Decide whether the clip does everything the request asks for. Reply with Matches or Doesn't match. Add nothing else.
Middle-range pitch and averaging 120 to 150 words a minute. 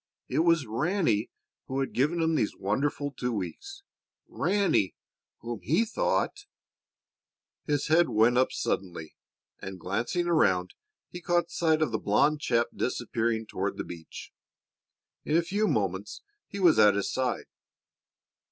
Doesn't match